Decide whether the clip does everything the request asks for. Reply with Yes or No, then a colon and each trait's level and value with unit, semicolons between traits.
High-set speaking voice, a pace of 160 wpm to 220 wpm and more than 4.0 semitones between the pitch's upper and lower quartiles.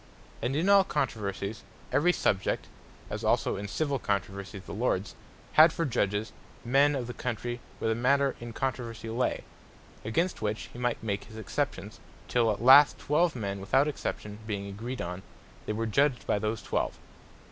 No: low, 115 Hz; average, 170 wpm; average, 4.9 semitones